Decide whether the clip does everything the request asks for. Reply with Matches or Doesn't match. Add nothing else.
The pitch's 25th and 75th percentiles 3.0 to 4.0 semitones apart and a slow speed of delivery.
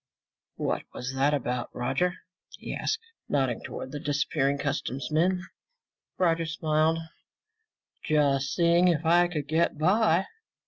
Matches